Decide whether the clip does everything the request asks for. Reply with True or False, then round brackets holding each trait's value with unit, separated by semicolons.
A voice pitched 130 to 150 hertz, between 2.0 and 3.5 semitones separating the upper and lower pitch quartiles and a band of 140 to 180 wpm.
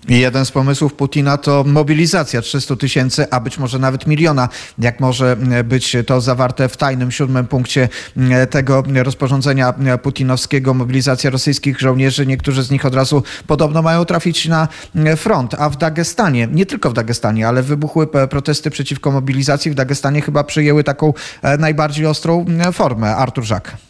True (140 Hz; 2.8 semitones; 150 wpm)